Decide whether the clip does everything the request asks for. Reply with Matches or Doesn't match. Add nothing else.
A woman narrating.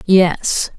Matches